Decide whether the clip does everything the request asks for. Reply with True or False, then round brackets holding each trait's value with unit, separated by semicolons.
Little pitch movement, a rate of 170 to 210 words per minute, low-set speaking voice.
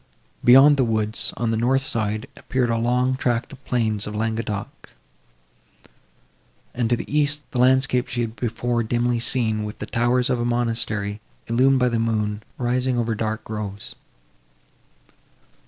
False (2.3 semitones; 155 wpm; 120 Hz)